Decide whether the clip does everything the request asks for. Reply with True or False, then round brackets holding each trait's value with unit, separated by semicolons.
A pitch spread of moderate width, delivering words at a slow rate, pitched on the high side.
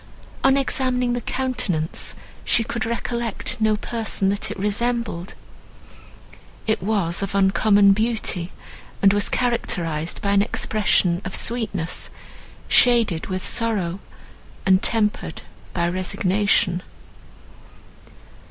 True (3.9 semitones; 105 wpm; 205 Hz)